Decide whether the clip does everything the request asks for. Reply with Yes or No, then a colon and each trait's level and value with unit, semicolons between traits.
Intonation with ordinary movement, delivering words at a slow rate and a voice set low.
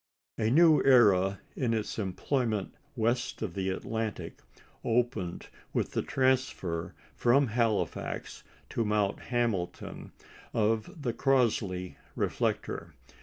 Yes: average, 4.1 semitones; slow, 105 wpm; low, 115 Hz